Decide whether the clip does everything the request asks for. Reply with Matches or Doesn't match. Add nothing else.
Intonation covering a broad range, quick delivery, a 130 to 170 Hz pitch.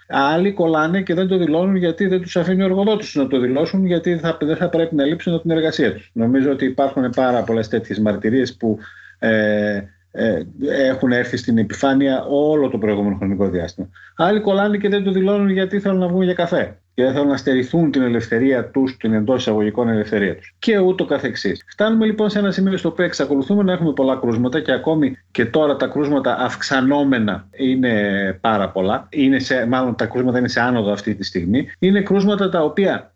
Matches